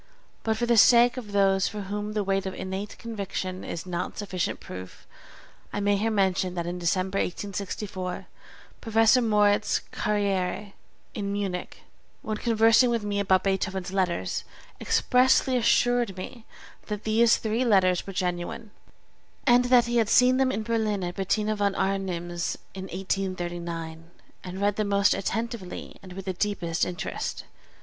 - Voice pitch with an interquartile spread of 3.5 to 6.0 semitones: No, average, 3.0 semitones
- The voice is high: Yes, high, 200 Hz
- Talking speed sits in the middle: Yes, average, 150 wpm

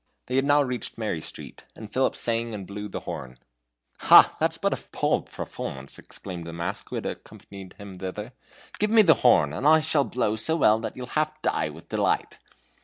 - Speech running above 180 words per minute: Yes, average, 195 wpm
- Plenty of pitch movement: Yes, wide, 6.4 semitones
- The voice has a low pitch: Yes, low, 110 Hz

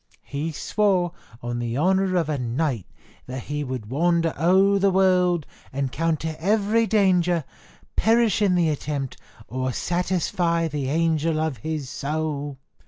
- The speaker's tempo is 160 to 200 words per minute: No, slow, 135 wpm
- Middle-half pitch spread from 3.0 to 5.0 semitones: Yes, average, 4.4 semitones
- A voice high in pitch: No, medium, 160 Hz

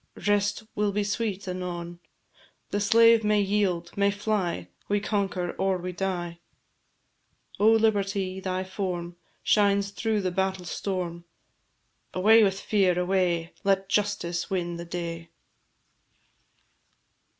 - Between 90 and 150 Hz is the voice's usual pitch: No, high, 190 Hz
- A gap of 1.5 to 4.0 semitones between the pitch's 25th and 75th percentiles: Yes, narrow, 2.6 semitones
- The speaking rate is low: Yes, slow, 115 wpm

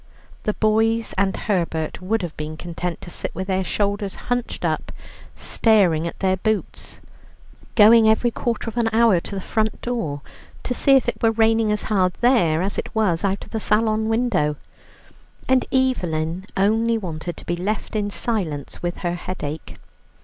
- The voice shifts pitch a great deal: No, average, 4.3 semitones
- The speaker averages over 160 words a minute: Yes, average, 170 wpm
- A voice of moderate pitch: No, high, 205 Hz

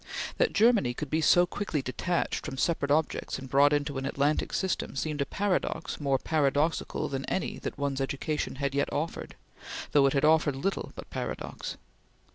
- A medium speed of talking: Yes, average, 175 wpm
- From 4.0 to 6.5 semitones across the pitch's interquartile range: No, average, 2.7 semitones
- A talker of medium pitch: Yes, medium, 145 Hz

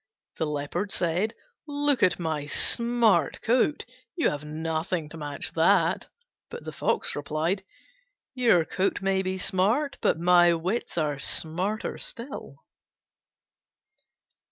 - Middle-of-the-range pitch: Yes, medium, 180 Hz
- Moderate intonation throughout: No, wide, 5.8 semitones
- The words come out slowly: Yes, slow, 120 wpm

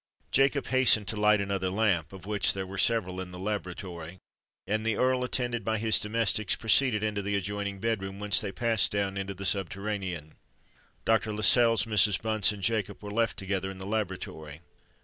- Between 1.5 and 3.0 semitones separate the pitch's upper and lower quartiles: Yes, narrow, 2.5 semitones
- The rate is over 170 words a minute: Yes, average, 185 wpm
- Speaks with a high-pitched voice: No, low, 105 Hz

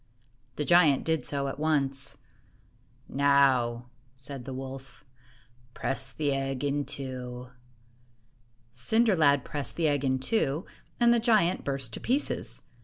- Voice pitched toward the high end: No, medium, 140 Hz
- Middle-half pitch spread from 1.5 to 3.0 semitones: Yes, average, 2.7 semitones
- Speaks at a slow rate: Yes, slow, 130 wpm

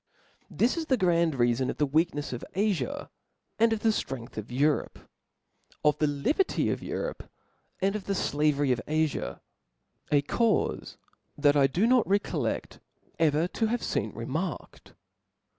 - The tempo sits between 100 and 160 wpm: Yes, average, 150 wpm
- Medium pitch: Yes, medium, 155 Hz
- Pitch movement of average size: No, wide, 7.0 semitones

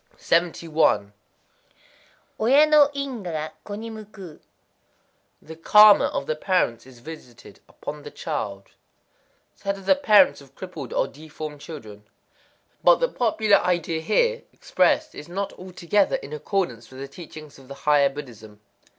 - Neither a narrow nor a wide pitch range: No, wide, 6.8 semitones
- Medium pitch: Yes, medium, 165 Hz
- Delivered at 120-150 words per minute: Yes, average, 140 wpm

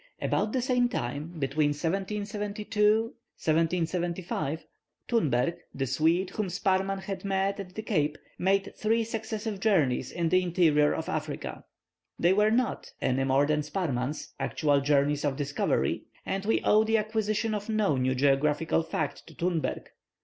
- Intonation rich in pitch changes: Yes, wide, 6.0 semitones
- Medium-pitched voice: Yes, medium, 180 Hz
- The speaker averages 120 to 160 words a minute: Yes, average, 145 wpm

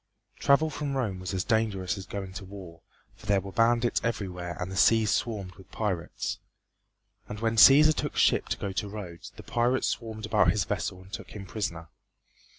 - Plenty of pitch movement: No, average, 3.5 semitones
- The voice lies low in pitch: Yes, low, 100 Hz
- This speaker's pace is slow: No, average, 190 wpm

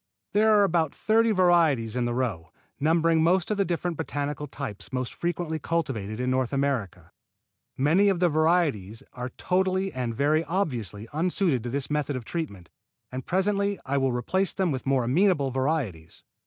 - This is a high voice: No, medium, 150 Hz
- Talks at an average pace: Yes, average, 170 wpm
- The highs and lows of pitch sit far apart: Yes, wide, 5.7 semitones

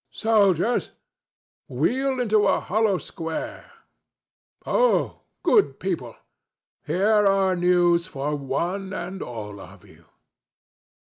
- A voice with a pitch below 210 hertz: Yes, high, 190 Hz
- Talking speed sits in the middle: No, slow, 90 wpm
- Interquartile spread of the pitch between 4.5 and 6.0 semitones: Yes, average, 4.8 semitones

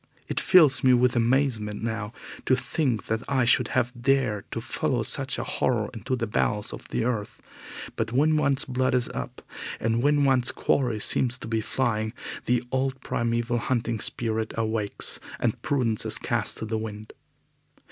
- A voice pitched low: Yes, low, 120 Hz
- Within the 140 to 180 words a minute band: Yes, average, 170 wpm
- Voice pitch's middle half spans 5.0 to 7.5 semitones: No, average, 2.8 semitones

